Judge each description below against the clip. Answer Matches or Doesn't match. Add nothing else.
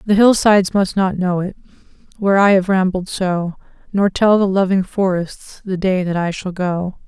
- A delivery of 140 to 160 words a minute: Doesn't match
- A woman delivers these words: Matches